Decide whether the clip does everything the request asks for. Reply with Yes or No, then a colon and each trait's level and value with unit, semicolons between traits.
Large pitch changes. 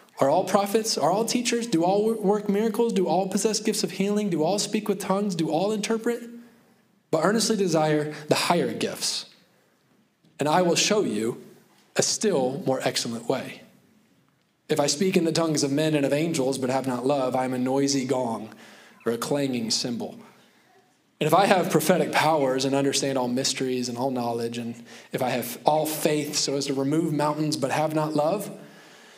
Yes: wide, 6.8 semitones